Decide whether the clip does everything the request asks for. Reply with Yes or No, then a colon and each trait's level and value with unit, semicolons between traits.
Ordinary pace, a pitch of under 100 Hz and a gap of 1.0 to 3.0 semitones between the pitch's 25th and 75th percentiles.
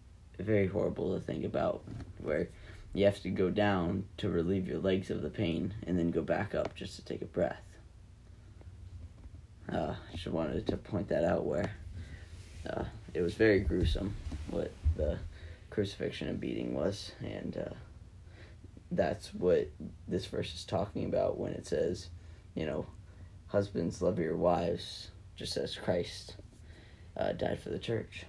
Yes: average, 155 wpm; very low, 90 Hz; narrow, 2.4 semitones